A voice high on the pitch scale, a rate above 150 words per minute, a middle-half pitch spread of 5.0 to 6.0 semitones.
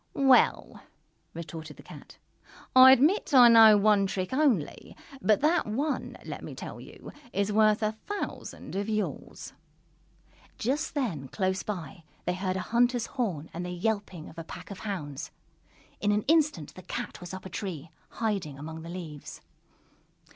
Yes: high, 200 Hz; average, 160 wpm; wide, 5.4 semitones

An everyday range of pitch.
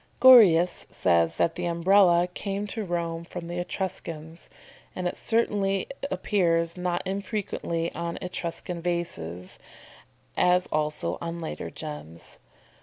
No: narrow, 2.3 semitones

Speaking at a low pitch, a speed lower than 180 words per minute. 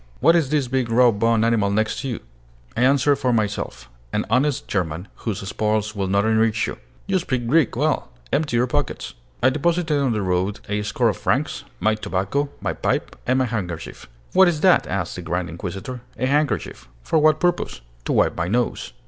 No: low, 115 Hz; average, 190 wpm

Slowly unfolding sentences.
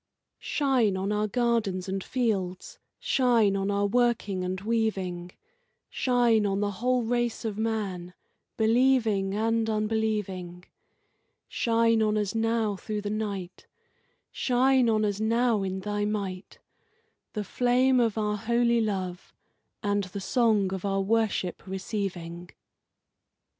Yes: slow, 125 wpm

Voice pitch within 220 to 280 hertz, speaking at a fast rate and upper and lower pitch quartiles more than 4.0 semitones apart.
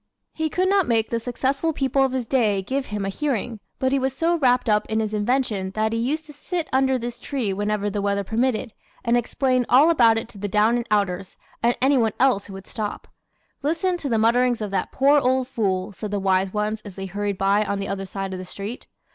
Yes: high, 230 Hz; fast, 240 wpm; average, 4.5 semitones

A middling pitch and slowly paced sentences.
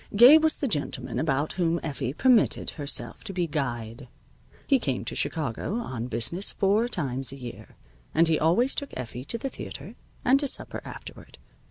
No: medium, 160 Hz; average, 175 wpm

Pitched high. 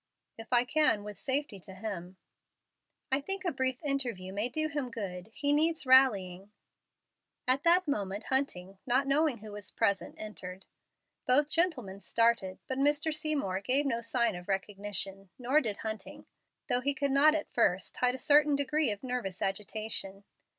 Yes: high, 240 Hz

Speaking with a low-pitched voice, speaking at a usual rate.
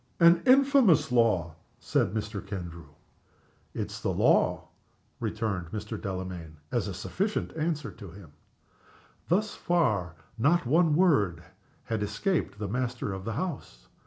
No: low, 110 Hz; slow, 130 wpm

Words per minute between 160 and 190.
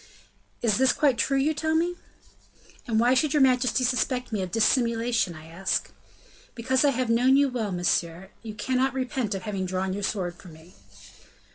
Yes: average, 180 wpm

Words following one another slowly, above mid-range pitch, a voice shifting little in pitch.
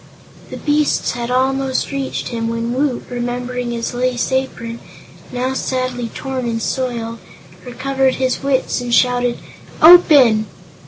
Yes: slow, 125 wpm; very high, 250 Hz; narrow, 1.8 semitones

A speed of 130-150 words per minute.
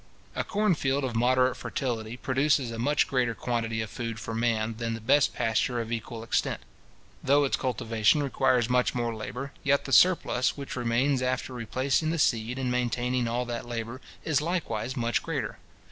No: average, 175 wpm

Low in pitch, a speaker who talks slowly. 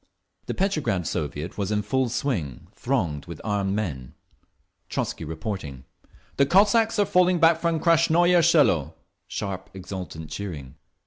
Yes: low, 105 Hz; slow, 130 wpm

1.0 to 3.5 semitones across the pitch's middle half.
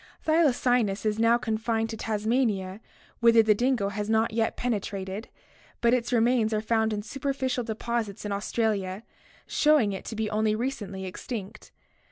Yes: narrow, 2.4 semitones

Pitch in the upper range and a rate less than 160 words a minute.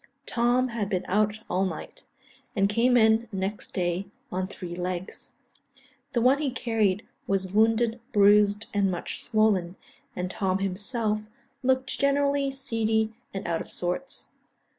Yes: high, 210 Hz; average, 140 wpm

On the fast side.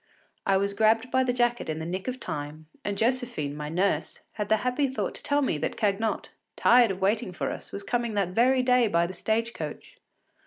Yes: fast, 220 wpm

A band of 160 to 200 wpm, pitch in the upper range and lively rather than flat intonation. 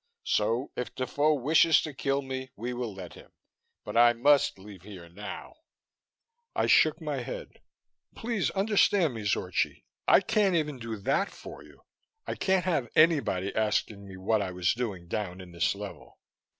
No: average, 165 wpm; low, 120 Hz; wide, 7.2 semitones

